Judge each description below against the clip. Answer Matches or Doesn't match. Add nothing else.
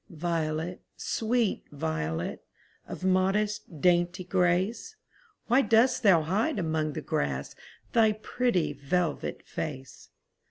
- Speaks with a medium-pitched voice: Matches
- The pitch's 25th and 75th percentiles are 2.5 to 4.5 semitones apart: Doesn't match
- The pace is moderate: Doesn't match